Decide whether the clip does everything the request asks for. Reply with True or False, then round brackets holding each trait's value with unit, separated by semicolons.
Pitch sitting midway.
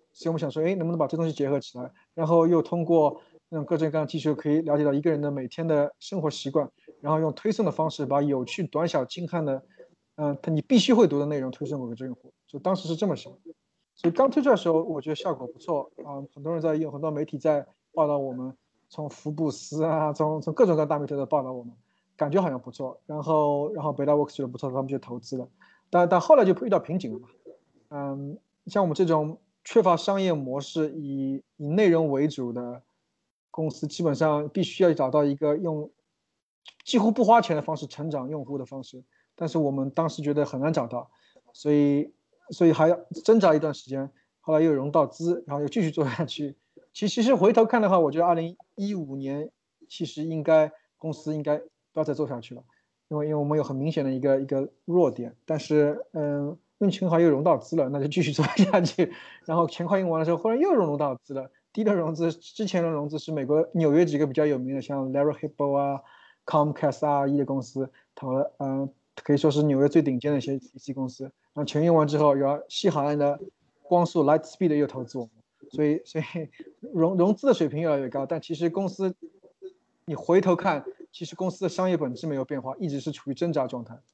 True (155 Hz)